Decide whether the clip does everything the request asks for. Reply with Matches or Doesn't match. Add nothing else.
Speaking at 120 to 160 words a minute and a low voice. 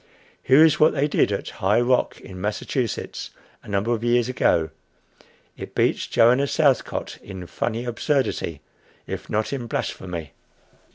Matches